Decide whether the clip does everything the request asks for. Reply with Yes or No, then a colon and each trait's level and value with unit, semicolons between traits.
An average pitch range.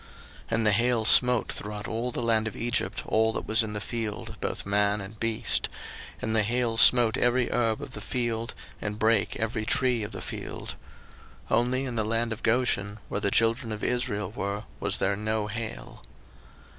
No: narrow, 2.1 semitones